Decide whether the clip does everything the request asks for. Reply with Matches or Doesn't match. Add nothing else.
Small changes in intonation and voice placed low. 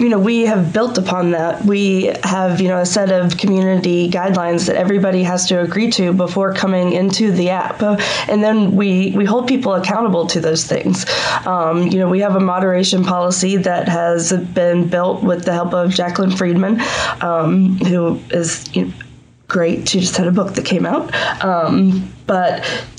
Doesn't match